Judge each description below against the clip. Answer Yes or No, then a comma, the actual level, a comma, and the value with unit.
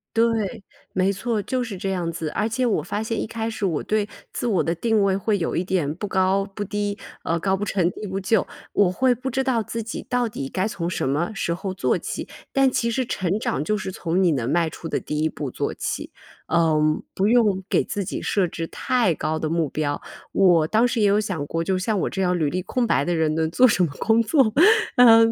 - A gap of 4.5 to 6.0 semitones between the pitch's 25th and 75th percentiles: Yes, average, 4.8 semitones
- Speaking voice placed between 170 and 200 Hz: Yes, high, 195 Hz